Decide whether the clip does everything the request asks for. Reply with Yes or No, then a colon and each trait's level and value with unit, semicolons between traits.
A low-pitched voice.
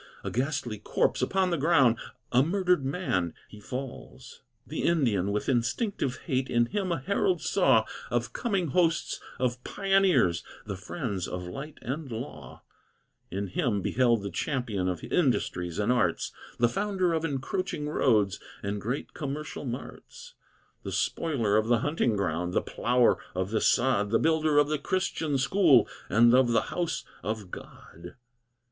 Yes: low, 125 Hz